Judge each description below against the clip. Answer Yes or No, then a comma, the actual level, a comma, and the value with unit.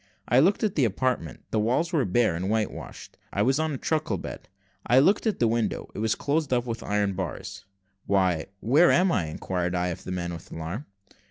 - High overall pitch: No, low, 110 Hz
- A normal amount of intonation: No, wide, 7.4 semitones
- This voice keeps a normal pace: No, fast, 220 wpm